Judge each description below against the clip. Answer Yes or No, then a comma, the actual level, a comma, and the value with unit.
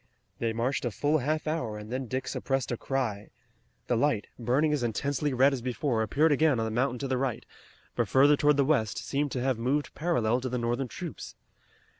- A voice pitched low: Yes, low, 130 Hz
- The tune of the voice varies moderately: Yes, average, 3.4 semitones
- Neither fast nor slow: No, fast, 210 wpm